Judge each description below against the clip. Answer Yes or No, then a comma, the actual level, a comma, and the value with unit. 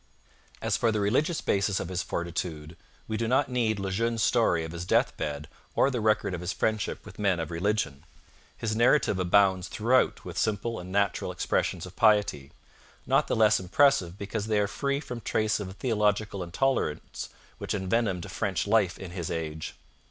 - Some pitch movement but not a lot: Yes, average, 4.0 semitones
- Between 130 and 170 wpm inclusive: No, average, 180 wpm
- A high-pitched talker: No, low, 100 Hz